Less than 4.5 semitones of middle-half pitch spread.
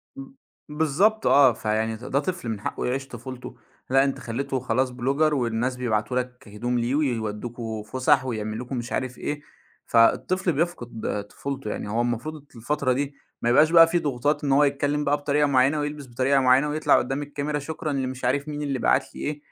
Yes: average, 3.4 semitones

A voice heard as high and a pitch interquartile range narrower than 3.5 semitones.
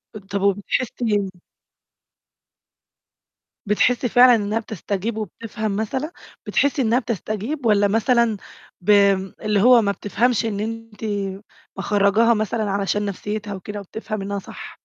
Yes: high, 215 Hz; narrow, 2.4 semitones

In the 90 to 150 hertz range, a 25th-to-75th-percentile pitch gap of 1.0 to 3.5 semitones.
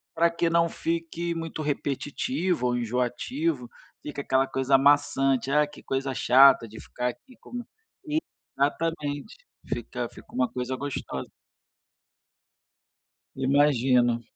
No: medium, 140 Hz; average, 4.4 semitones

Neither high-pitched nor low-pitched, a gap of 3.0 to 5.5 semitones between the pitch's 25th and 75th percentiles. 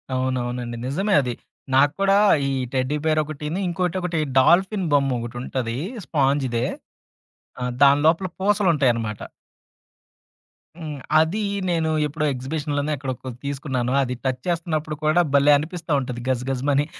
Yes: medium, 145 Hz; average, 4.1 semitones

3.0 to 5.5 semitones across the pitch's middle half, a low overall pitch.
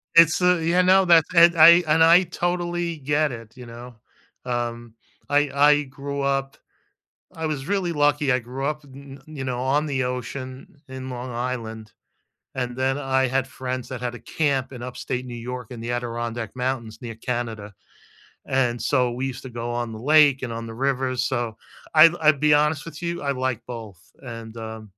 Yes: average, 3.6 semitones; low, 130 Hz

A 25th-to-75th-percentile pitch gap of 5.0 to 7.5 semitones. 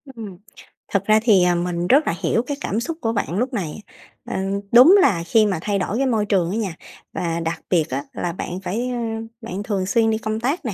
No: average, 4.5 semitones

